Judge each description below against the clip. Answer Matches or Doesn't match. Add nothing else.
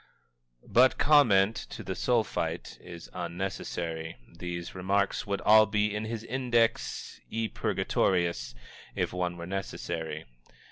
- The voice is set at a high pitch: Doesn't match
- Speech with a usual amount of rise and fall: Matches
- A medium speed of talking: Doesn't match